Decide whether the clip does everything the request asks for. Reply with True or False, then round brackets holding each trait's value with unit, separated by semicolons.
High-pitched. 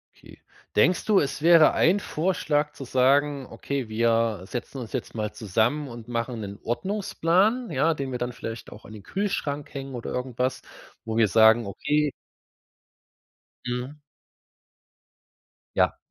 False (130 Hz)